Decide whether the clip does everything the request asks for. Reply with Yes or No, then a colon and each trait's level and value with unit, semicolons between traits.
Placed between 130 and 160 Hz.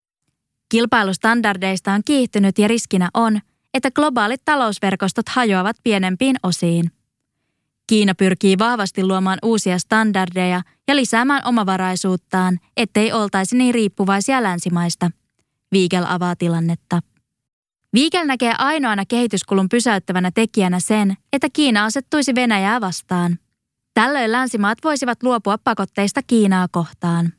No: high, 205 Hz